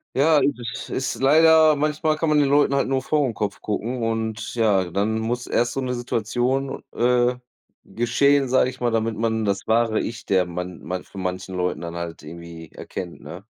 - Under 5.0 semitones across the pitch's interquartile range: No, wide, 5.4 semitones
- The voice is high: No, low, 115 Hz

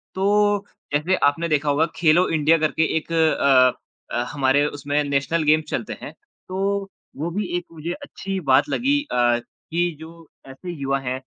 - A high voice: No, medium, 160 Hz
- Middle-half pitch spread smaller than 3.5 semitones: No, average, 4.7 semitones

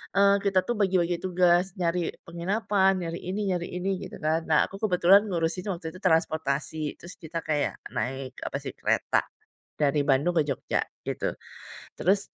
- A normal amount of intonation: Yes, average, 3.0 semitones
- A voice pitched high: No, medium, 175 Hz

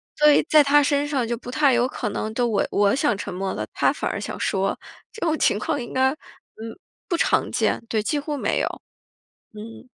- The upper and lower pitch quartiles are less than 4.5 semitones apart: No, average, 5.2 semitones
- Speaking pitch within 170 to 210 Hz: No, very high, 250 Hz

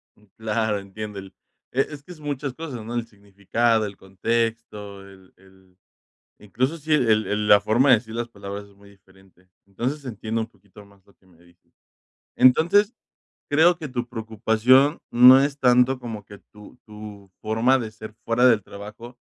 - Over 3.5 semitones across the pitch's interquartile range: Yes, average, 3.9 semitones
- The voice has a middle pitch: No, low, 110 Hz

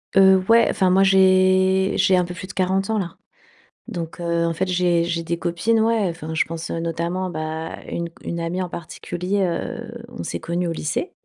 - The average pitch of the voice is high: No, medium, 180 Hz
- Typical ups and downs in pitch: No, narrow, 2.2 semitones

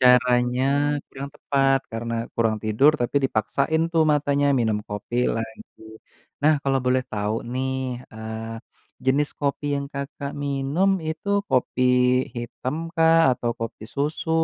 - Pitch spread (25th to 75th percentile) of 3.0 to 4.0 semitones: Yes, average, 3.7 semitones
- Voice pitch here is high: No, low, 130 Hz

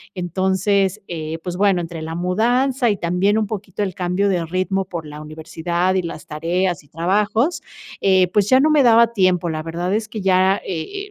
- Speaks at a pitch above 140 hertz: Yes, medium, 185 Hz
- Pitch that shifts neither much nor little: Yes, average, 3.2 semitones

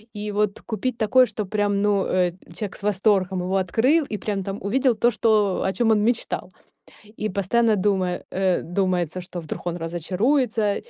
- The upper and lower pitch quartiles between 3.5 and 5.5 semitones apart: No, average, 2.9 semitones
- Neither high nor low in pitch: No, high, 205 Hz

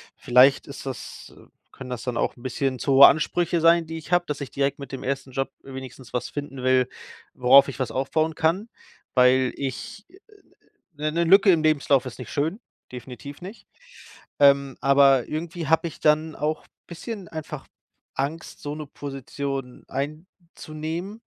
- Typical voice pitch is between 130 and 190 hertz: Yes, medium, 140 Hz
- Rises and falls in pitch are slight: No, average, 3.3 semitones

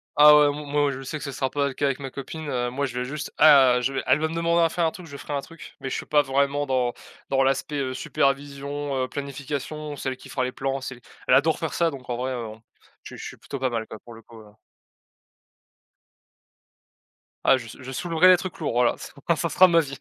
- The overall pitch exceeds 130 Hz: Yes, medium, 140 Hz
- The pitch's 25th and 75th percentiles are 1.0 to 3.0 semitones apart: Yes, narrow, 2.4 semitones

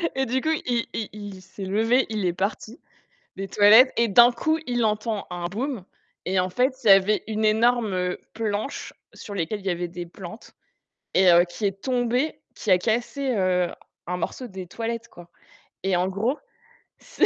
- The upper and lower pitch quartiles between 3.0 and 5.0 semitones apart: Yes, average, 4.2 semitones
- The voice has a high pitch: Yes, high, 210 Hz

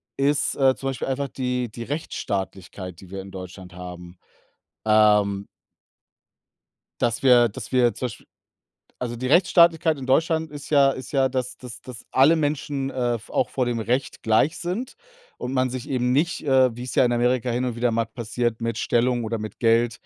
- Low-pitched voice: Yes, low, 125 Hz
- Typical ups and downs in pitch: Yes, average, 3.1 semitones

